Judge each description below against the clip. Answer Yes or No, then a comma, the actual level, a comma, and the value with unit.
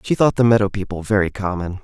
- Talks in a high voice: No, low, 100 Hz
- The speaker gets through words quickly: Yes, fast, 230 wpm